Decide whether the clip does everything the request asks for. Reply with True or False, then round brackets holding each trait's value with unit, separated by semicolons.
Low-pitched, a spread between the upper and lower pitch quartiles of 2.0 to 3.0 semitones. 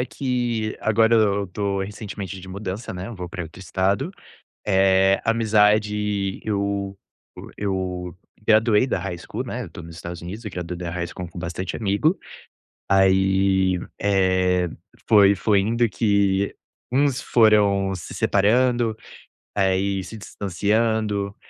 True (100 Hz; 2.4 semitones)